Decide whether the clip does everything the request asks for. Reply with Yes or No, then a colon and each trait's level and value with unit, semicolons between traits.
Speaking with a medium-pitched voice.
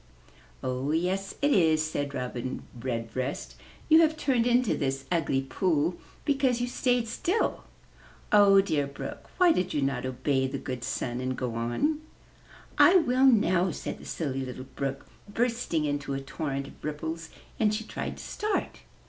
Yes: medium, 155 Hz